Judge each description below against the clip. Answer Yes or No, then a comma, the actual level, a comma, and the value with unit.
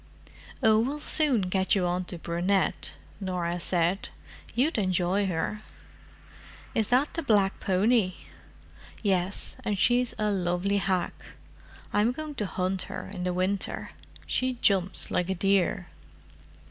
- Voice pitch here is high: Yes, high, 195 Hz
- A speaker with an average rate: No, slow, 130 wpm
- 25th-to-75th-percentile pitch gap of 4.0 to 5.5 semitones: No, average, 3.3 semitones